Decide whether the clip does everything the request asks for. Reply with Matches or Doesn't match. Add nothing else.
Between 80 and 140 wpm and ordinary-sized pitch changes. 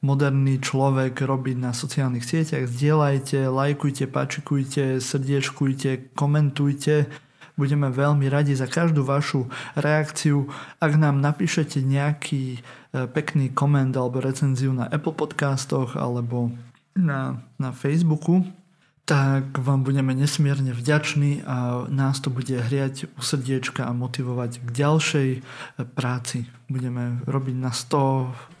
Doesn't match